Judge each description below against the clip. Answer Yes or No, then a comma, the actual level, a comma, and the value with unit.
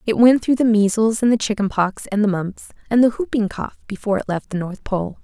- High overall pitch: Yes, high, 215 Hz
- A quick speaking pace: Yes, fast, 250 wpm